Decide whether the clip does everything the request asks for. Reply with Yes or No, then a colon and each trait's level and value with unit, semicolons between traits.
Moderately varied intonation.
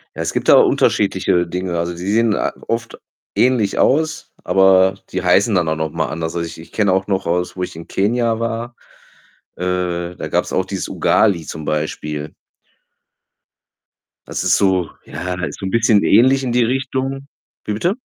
Yes: average, 5.0 semitones